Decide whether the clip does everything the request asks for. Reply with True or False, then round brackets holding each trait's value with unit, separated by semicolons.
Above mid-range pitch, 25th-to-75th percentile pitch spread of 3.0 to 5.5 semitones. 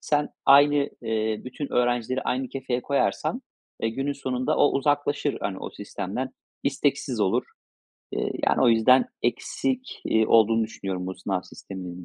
False (125 Hz; 3.9 semitones)